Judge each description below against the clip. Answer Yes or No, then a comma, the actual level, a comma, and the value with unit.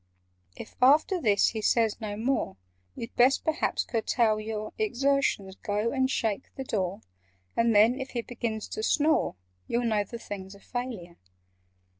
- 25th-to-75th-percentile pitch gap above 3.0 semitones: Yes, average, 3.8 semitones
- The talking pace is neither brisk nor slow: Yes, average, 150 wpm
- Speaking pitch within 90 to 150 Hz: No, high, 230 Hz